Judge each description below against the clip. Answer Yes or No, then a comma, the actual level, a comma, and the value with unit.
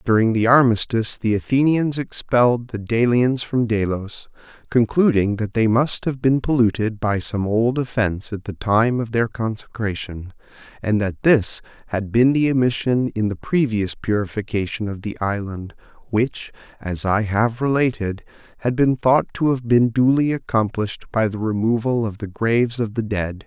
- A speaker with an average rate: Yes, average, 160 wpm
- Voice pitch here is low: Yes, low, 115 Hz